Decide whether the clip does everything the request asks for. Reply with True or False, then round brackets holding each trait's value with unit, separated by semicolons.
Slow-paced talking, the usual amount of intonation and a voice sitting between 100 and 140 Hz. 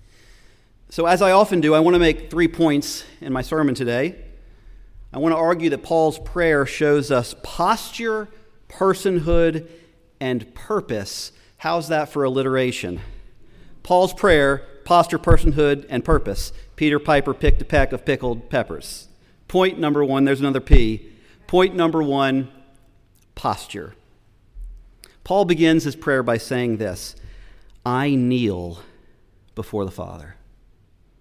False (130 wpm; 7.0 semitones; 135 Hz)